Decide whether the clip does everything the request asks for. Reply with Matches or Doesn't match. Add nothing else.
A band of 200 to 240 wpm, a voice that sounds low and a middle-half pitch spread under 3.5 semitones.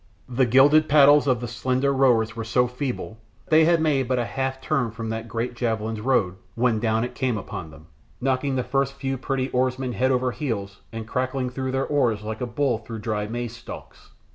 Matches